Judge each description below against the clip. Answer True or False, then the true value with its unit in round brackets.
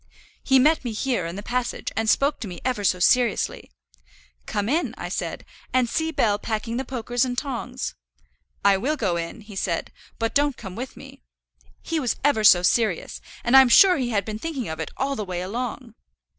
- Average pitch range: True (4.6 semitones)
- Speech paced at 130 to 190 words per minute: False (200 wpm)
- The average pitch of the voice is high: True (235 Hz)